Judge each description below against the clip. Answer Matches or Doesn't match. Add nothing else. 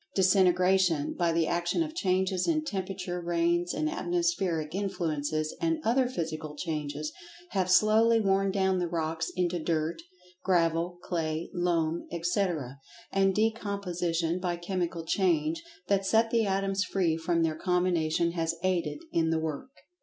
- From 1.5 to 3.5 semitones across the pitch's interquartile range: Matches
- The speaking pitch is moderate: Matches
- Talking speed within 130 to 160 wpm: Matches